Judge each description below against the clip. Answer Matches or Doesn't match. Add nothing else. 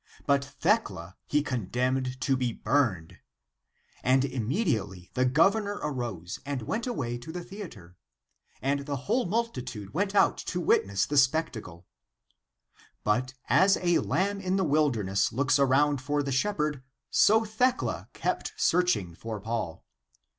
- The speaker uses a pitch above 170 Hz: Doesn't match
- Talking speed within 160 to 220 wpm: Doesn't match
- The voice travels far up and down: Matches